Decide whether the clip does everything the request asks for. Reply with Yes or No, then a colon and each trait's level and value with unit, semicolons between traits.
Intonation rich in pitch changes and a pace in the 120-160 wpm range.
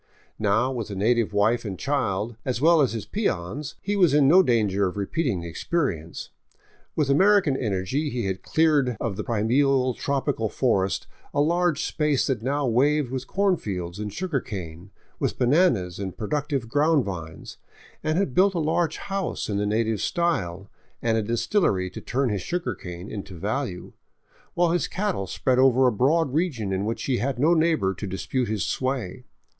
No: wide, 6.8 semitones; average, 180 wpm